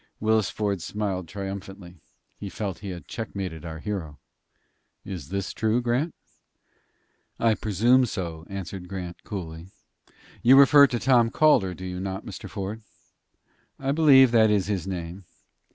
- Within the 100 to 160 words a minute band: Yes, average, 145 wpm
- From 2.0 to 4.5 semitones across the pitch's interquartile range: Yes, average, 3.8 semitones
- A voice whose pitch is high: No, low, 100 Hz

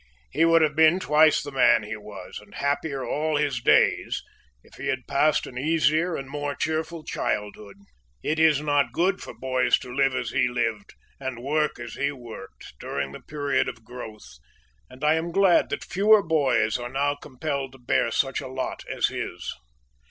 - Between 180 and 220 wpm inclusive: Yes, average, 190 wpm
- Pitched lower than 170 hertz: Yes, medium, 140 Hz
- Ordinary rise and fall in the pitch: Yes, average, 4.0 semitones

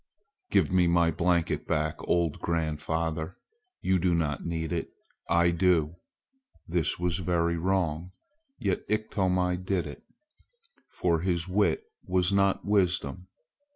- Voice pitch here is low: Yes, very low, 85 Hz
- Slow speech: Yes, slow, 120 wpm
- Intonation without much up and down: Yes, narrow, 2.0 semitones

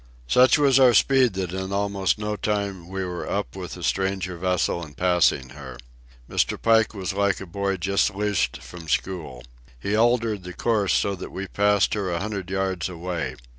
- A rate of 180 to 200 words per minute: Yes, average, 185 wpm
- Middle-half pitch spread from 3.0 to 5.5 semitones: No, narrow, 2.6 semitones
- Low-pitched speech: Yes, very low, 95 Hz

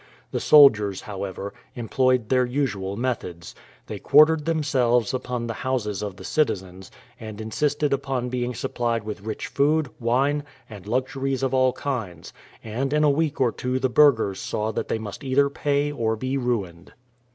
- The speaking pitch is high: No, low, 125 Hz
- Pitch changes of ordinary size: Yes, average, 4.4 semitones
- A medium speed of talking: Yes, average, 165 wpm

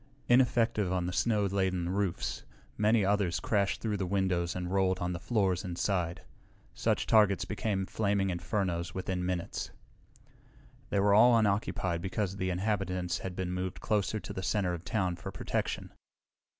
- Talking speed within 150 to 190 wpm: Yes, average, 155 wpm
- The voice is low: Yes, very low, 95 Hz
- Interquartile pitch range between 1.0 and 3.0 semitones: Yes, narrow, 2.4 semitones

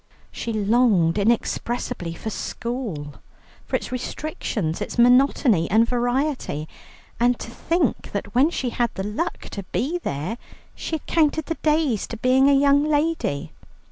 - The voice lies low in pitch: No, high, 245 Hz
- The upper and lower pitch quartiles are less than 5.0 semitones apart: No, wide, 5.5 semitones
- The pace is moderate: Yes, average, 145 wpm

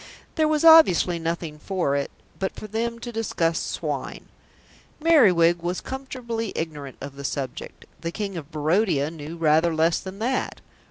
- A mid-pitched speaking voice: Yes, medium, 175 Hz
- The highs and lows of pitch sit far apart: Yes, wide, 6.1 semitones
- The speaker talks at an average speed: Yes, average, 155 wpm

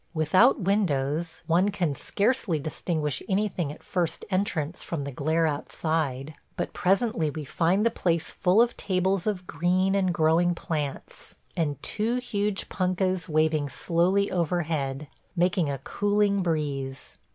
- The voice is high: No, medium, 175 Hz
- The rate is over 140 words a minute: No, slow, 135 wpm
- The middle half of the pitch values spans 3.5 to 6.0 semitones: Yes, average, 3.9 semitones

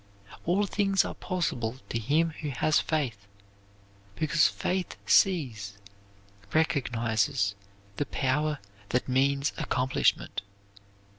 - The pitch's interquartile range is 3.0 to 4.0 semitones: No, average, 5.1 semitones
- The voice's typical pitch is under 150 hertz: Yes, medium, 140 Hz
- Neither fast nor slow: No, slow, 95 wpm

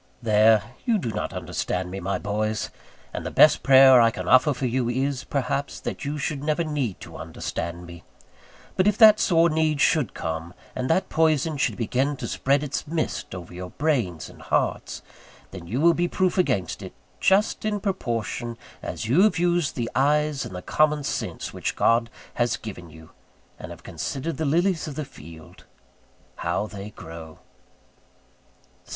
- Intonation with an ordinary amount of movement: No, wide, 7.1 semitones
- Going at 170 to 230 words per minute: Yes, average, 175 wpm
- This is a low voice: Yes, low, 130 Hz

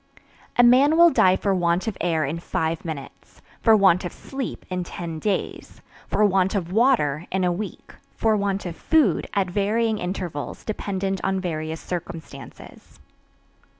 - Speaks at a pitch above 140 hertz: Yes, high, 190 Hz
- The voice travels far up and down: No, average, 3.8 semitones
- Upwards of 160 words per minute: No, average, 155 wpm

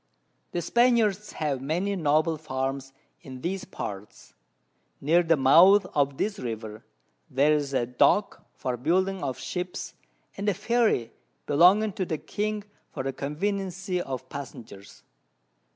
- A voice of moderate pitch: Yes, medium, 160 Hz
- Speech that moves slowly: Yes, slow, 130 wpm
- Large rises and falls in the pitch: Yes, wide, 6.4 semitones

